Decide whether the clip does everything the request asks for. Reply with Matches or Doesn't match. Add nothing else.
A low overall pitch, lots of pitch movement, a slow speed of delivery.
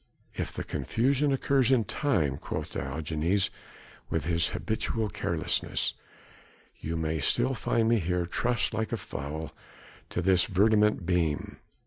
Matches